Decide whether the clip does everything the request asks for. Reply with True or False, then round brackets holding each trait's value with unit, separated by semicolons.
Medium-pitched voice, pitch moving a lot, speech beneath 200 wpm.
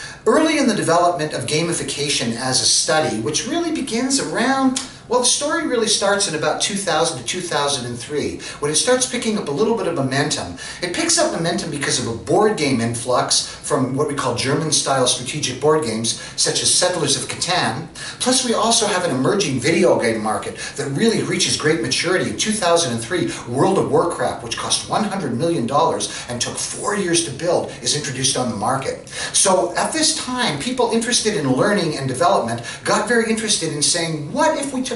True (165 Hz; 8.7 semitones; 190 wpm)